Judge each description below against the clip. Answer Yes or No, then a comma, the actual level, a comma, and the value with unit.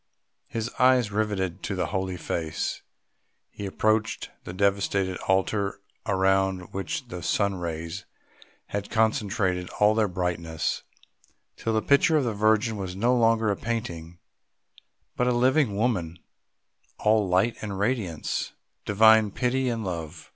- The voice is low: Yes, low, 100 Hz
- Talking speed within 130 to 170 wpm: Yes, slow, 135 wpm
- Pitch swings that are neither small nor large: Yes, average, 3.4 semitones